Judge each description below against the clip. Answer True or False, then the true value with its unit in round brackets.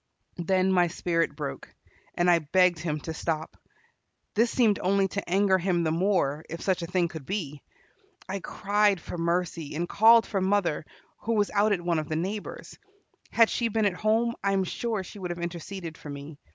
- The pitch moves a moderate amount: True (3.4 semitones)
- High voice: False (180 Hz)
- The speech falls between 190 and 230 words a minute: True (195 wpm)